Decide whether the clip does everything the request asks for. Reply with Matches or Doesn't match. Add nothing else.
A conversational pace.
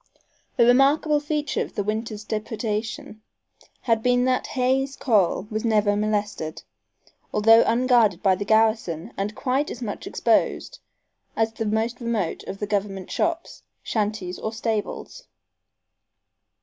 Doesn't match